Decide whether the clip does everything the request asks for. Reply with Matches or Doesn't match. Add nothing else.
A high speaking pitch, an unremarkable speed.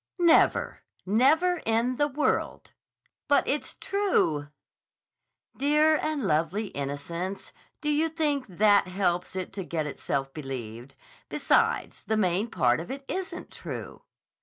Doesn't match